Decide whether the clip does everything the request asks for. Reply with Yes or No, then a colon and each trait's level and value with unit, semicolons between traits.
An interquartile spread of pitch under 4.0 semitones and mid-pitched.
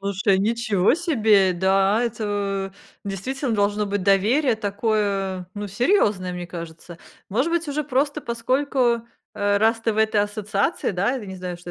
No: average, 3.3 semitones; high, 205 Hz